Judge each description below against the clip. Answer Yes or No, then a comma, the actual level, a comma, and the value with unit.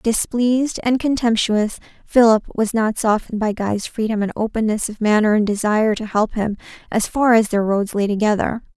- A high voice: Yes, high, 220 Hz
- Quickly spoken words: No, average, 180 wpm